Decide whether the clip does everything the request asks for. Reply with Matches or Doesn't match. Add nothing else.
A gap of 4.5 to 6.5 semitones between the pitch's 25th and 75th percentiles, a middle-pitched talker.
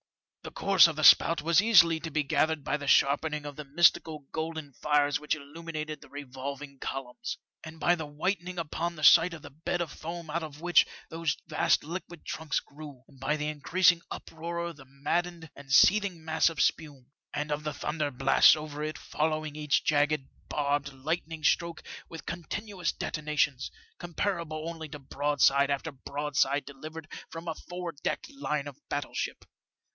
Doesn't match